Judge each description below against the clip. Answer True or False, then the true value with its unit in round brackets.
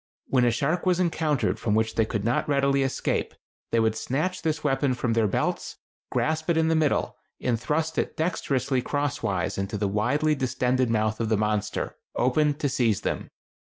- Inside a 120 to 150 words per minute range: False (185 wpm)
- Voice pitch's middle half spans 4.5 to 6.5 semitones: True (5.2 semitones)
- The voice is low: True (130 Hz)